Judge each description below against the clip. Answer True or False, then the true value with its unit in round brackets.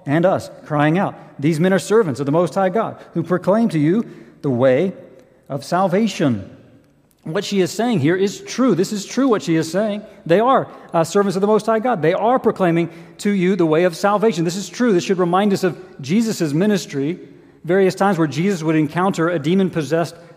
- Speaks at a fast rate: True (210 wpm)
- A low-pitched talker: False (185 Hz)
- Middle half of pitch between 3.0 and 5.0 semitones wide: True (3.5 semitones)